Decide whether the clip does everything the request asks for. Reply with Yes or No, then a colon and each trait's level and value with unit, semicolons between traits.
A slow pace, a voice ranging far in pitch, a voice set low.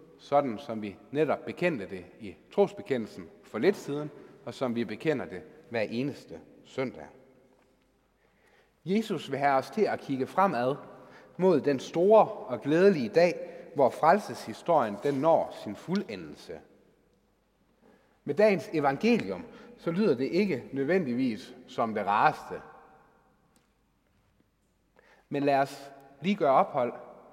No: slow, 125 wpm; wide, 6.6 semitones; medium, 155 Hz